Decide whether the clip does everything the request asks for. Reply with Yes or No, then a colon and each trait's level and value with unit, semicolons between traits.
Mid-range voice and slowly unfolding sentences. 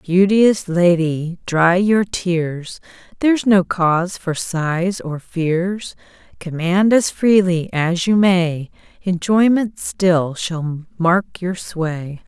Yes: medium, 180 Hz; slow, 115 wpm